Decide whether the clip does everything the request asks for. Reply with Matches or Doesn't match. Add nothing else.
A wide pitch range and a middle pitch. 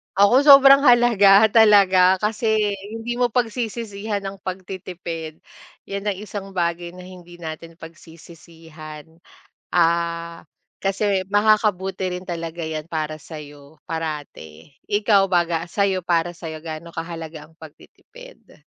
Doesn't match